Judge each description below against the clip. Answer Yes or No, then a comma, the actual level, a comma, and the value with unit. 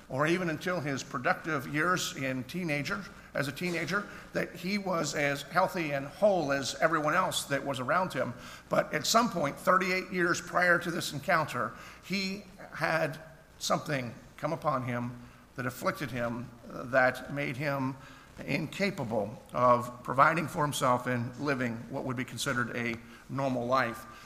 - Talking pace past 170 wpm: No, average, 150 wpm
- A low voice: No, medium, 145 Hz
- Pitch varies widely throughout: No, average, 4.9 semitones